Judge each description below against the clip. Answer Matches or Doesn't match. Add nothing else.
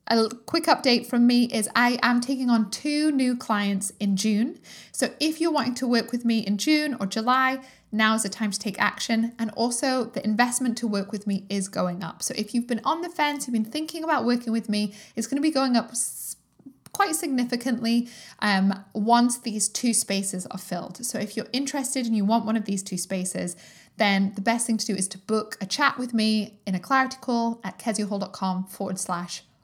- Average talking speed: Doesn't match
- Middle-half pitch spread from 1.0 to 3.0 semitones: Doesn't match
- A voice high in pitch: Matches